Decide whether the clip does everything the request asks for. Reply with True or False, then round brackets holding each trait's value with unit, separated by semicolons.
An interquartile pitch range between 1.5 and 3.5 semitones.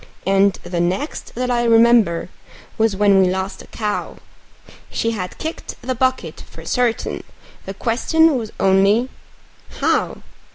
False (4.2 semitones)